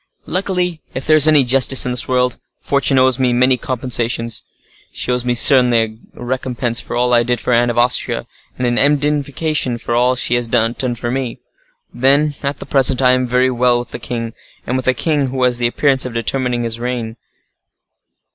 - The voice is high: No, low, 125 Hz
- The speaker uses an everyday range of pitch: No, narrow, 1.8 semitones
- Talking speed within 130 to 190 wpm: No, fast, 205 wpm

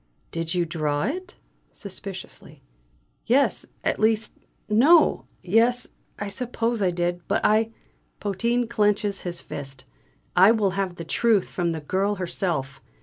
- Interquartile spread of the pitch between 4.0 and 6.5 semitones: Yes, average, 4.5 semitones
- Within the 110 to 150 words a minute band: Yes, average, 140 wpm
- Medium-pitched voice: No, high, 200 Hz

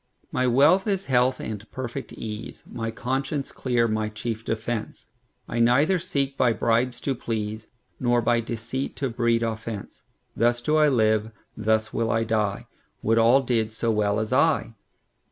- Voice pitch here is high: No, low, 115 Hz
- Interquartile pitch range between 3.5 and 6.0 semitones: No, narrow, 2.6 semitones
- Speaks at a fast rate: No, average, 145 wpm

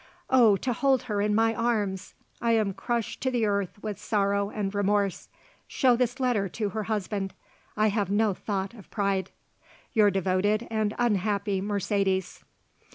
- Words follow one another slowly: No, average, 160 wpm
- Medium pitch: No, high, 205 Hz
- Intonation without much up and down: Yes, narrow, 2.3 semitones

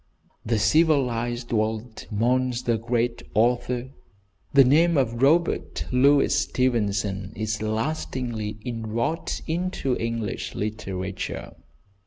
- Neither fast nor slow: No, slow, 95 wpm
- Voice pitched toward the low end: Yes, low, 120 Hz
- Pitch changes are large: No, average, 3.0 semitones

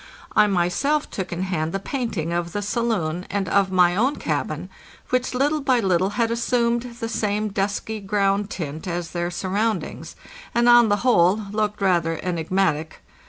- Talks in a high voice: Yes, high, 200 Hz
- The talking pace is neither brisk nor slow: Yes, average, 165 wpm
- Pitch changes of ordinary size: Yes, average, 4.6 semitones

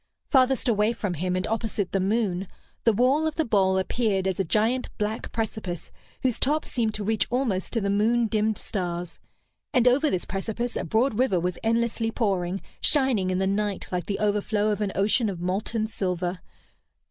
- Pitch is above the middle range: Yes, high, 210 Hz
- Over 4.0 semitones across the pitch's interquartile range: No, average, 3.5 semitones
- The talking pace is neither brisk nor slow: Yes, average, 185 wpm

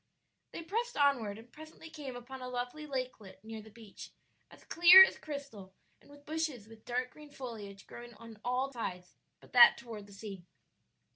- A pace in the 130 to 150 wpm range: No, average, 175 wpm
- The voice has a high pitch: Yes, high, 245 Hz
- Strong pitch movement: No, average, 4.8 semitones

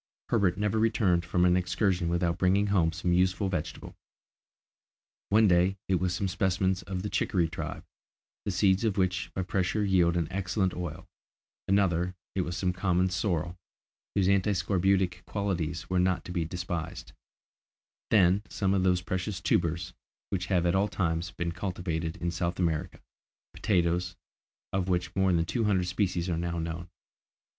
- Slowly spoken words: No, average, 160 wpm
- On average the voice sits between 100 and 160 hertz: No, very low, 90 Hz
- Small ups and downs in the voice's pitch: Yes, narrow, 1.8 semitones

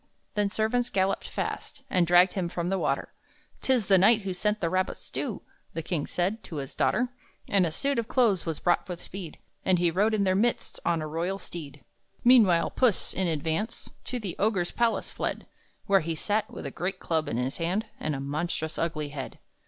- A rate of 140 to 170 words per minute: No, fast, 205 wpm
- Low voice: No, medium, 180 Hz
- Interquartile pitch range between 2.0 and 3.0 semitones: No, average, 4.3 semitones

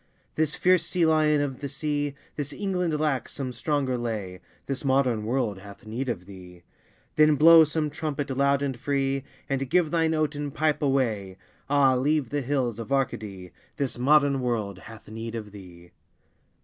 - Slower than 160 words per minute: No, average, 165 wpm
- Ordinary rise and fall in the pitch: Yes, average, 4.8 semitones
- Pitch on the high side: No, low, 135 Hz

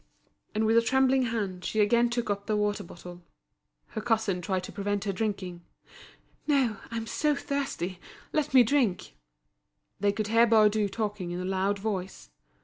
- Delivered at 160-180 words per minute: Yes, average, 165 wpm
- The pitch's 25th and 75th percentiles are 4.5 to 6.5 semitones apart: No, average, 3.3 semitones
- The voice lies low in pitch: No, high, 210 Hz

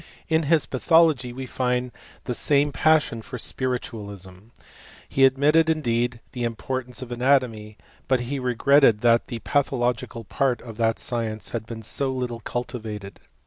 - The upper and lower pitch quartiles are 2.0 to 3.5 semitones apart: Yes, average, 2.8 semitones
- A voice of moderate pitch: No, low, 125 Hz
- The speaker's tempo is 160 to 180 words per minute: No, average, 145 wpm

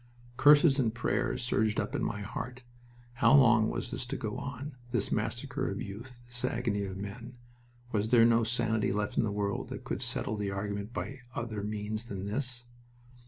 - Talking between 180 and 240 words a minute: Yes, average, 185 wpm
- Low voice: Yes, low, 115 Hz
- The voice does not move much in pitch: No, average, 3.2 semitones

